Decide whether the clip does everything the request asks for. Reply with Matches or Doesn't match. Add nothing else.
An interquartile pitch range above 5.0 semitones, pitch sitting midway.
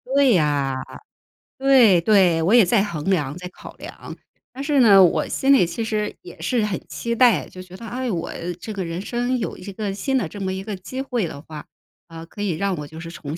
Doesn't match